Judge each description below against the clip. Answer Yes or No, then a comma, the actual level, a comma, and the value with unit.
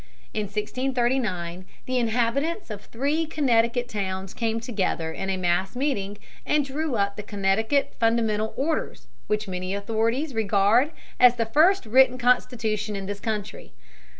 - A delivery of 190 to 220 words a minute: No, average, 140 wpm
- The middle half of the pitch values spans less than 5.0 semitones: Yes, average, 4.1 semitones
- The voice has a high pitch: Yes, high, 225 Hz